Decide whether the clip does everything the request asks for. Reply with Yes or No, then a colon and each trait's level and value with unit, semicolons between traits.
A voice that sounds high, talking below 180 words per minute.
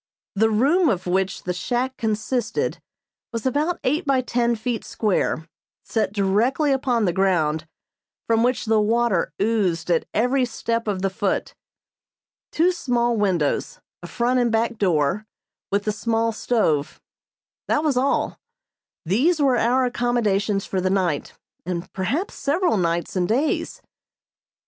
Yes: high, 225 Hz; average, 140 wpm